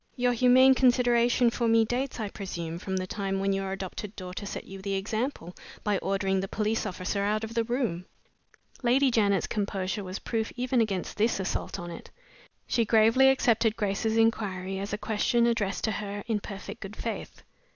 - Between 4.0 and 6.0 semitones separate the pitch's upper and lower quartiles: No, average, 3.2 semitones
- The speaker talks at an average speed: Yes, average, 180 wpm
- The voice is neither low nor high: No, high, 210 Hz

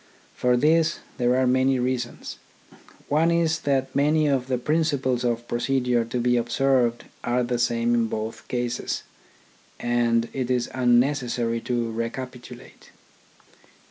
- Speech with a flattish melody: Yes, narrow, 2.1 semitones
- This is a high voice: No, low, 125 Hz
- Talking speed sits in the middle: No, slow, 130 wpm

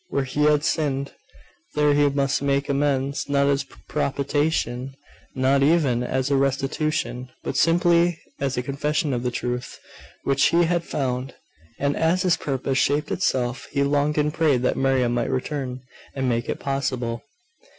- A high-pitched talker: No, medium, 140 Hz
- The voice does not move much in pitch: Yes, narrow, 2.2 semitones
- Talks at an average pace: Yes, average, 160 wpm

